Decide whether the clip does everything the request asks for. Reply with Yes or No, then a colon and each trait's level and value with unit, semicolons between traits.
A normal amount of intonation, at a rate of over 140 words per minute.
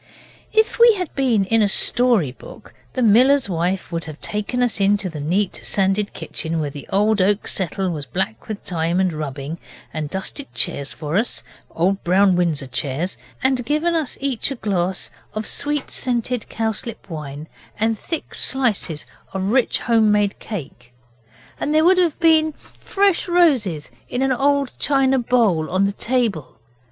No: wide, 7.2 semitones; average, 165 wpm